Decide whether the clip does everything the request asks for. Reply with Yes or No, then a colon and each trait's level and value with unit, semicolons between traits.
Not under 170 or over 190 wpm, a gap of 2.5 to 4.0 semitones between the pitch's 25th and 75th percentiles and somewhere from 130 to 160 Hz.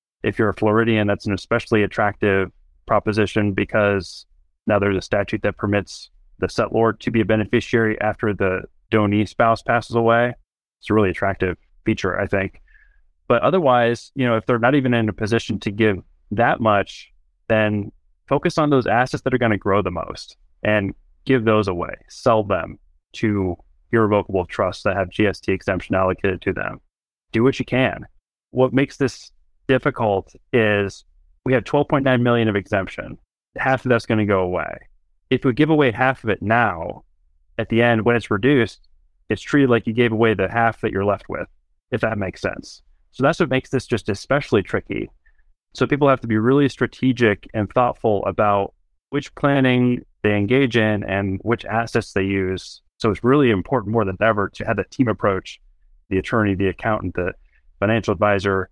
No: average, 180 wpm; average, 3.7 semitones; low, 105 Hz